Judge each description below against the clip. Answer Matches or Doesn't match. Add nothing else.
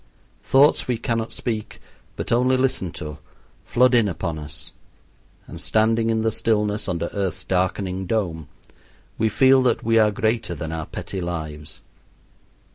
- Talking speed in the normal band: Matches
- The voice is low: Matches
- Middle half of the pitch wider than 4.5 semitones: Matches